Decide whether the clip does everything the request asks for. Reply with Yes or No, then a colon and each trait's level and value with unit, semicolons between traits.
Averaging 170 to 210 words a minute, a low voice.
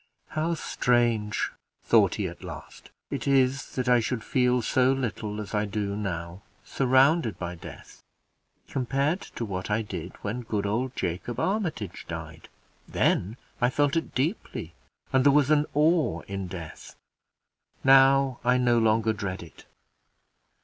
No: average, 145 wpm; low, 120 Hz